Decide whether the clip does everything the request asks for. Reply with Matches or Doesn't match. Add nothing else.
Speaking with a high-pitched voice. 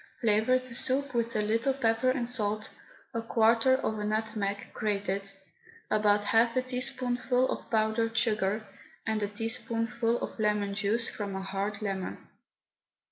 Matches